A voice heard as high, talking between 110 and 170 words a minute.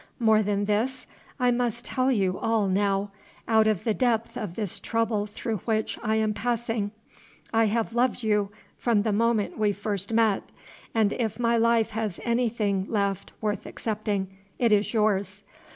Yes: high, 220 Hz; average, 165 wpm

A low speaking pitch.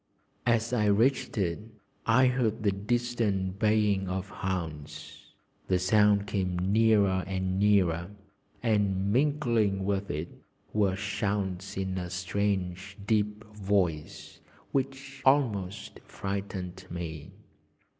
Yes: low, 100 Hz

